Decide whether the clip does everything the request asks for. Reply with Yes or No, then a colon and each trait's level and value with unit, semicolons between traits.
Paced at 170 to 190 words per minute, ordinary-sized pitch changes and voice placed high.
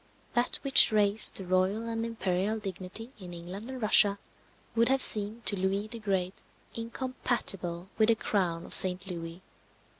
No: average, 155 wpm; average, 3.6 semitones; high, 205 Hz